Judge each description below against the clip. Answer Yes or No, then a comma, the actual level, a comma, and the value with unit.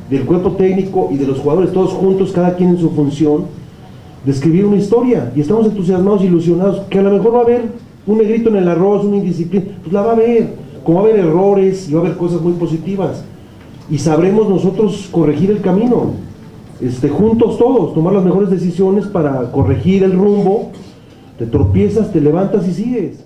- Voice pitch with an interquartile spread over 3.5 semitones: Yes, average, 4.2 semitones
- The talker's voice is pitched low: No, medium, 185 Hz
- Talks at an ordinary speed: No, fast, 195 wpm